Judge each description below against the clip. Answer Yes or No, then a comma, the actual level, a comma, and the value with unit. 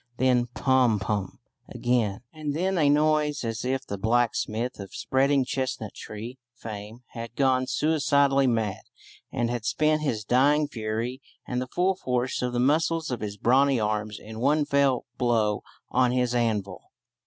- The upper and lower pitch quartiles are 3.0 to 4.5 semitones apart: Yes, average, 3.9 semitones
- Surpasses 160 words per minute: No, average, 155 wpm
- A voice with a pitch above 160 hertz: No, low, 125 Hz